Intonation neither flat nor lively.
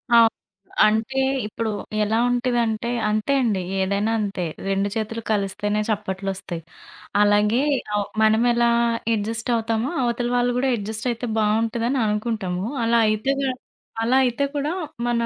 No: narrow, 2.3 semitones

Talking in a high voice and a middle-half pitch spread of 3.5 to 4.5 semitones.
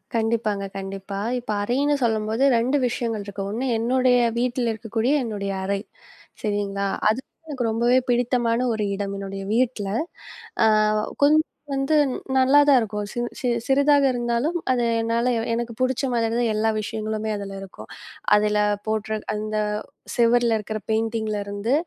No: high, 225 Hz; average, 2.7 semitones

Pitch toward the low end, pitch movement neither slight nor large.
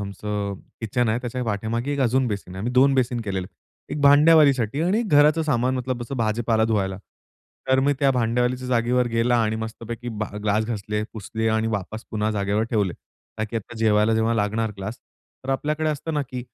Yes: low, 115 Hz; average, 3.3 semitones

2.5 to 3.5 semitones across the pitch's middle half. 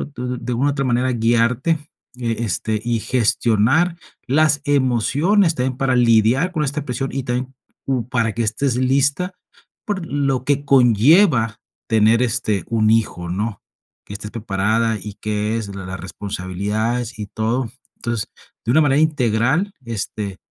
No: average, 3.9 semitones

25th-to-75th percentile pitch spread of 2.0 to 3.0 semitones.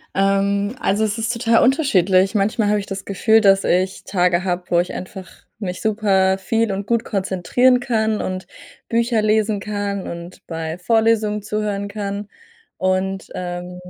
Yes: narrow, 2.6 semitones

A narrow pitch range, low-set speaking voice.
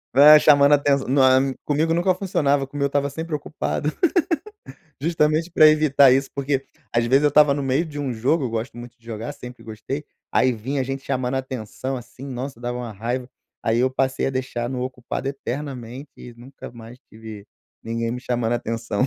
No: average, 3.0 semitones; low, 130 Hz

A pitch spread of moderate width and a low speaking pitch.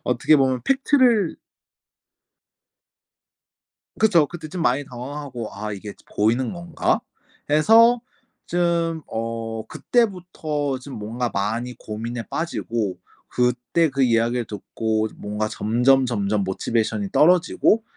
No: wide, 6.8 semitones; low, 125 Hz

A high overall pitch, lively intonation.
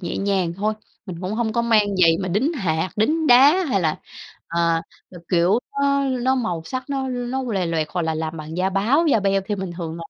Yes: high, 195 Hz; wide, 6.6 semitones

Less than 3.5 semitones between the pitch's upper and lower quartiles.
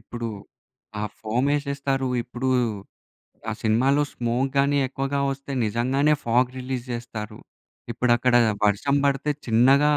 Yes: average, 2.8 semitones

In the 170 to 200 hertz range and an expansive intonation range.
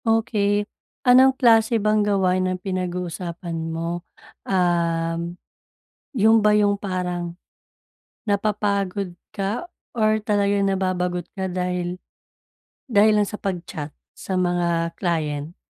No: medium, 185 Hz; average, 3.0 semitones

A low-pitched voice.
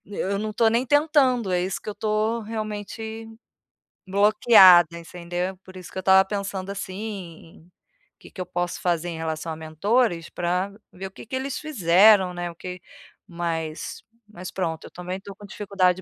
No: high, 190 Hz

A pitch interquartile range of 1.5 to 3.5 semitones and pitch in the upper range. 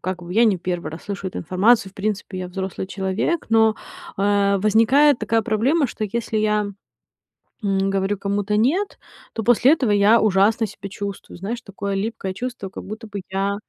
Yes: narrow, 2.5 semitones; high, 205 Hz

